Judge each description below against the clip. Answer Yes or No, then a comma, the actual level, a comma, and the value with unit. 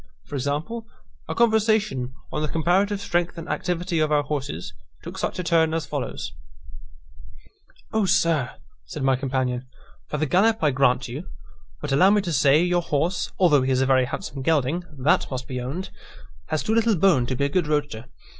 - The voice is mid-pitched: Yes, medium, 155 Hz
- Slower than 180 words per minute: No, average, 185 wpm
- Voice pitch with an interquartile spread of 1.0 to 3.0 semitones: No, average, 5.1 semitones